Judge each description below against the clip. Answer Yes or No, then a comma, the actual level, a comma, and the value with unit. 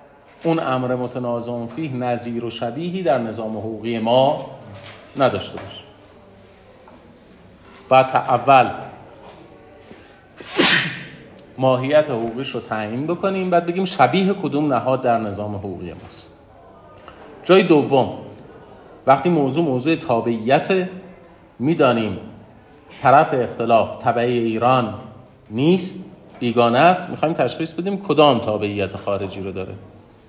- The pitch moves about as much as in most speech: No, wide, 6.2 semitones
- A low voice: Yes, low, 125 Hz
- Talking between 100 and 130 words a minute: Yes, slow, 105 wpm